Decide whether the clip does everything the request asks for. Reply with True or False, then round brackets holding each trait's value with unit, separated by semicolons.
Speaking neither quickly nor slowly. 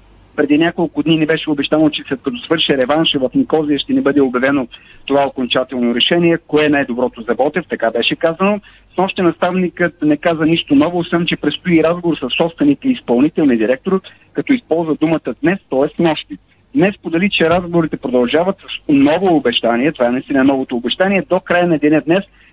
False (180 wpm)